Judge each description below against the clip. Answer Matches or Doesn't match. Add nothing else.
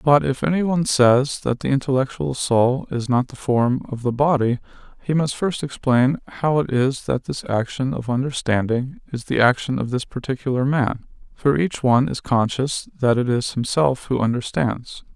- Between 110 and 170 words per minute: Doesn't match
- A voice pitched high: Doesn't match